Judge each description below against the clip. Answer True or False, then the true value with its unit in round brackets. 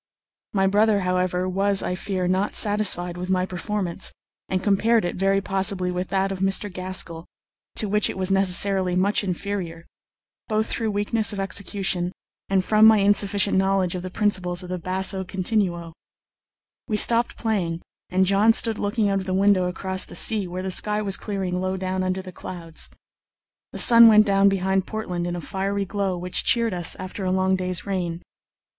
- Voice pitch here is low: False (190 Hz)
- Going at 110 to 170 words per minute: False (180 wpm)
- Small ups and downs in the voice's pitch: True (1.9 semitones)